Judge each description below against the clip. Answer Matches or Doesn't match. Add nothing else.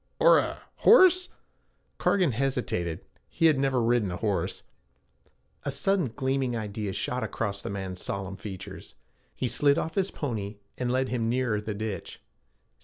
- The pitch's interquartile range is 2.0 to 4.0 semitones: Doesn't match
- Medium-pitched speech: Doesn't match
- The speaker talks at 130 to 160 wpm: Matches